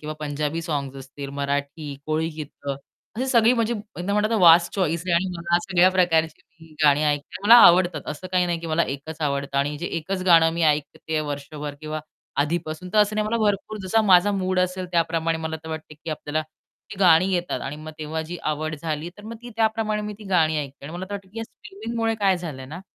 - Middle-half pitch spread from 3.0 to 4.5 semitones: Yes, average, 3.7 semitones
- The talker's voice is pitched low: No, medium, 165 Hz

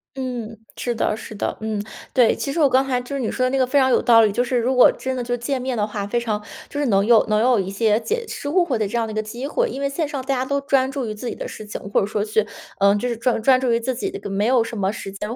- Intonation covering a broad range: No, average, 3.5 semitones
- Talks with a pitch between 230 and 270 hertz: Yes, high, 240 Hz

